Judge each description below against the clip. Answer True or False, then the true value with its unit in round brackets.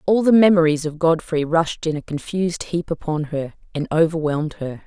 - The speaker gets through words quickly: False (185 wpm)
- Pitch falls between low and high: True (160 Hz)